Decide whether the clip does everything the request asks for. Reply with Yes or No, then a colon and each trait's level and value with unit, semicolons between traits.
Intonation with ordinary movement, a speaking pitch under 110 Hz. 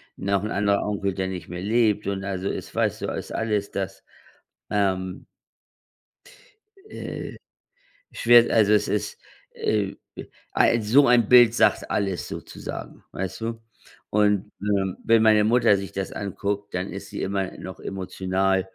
No: narrow, 1.9 semitones; low, 100 Hz